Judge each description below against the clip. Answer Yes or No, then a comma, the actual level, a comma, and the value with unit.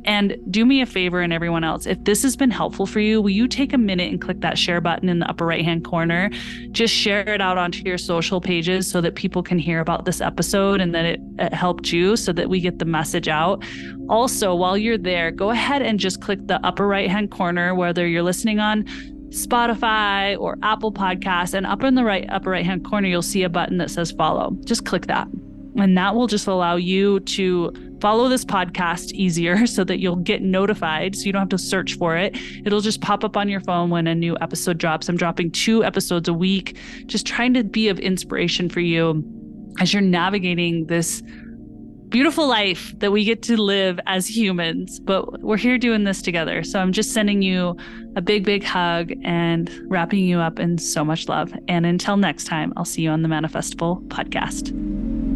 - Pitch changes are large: No, average, 3.6 semitones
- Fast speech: Yes, fast, 215 wpm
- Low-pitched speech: No, high, 190 Hz